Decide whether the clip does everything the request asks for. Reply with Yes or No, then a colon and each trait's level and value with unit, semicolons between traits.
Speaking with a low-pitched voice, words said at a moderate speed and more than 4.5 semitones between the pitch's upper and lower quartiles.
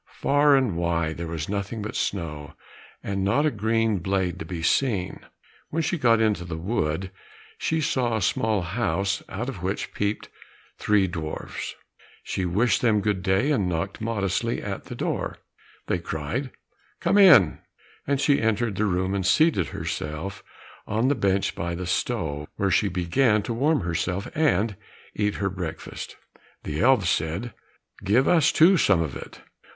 Yes: low, 100 Hz; average, 165 wpm; average, 5.1 semitones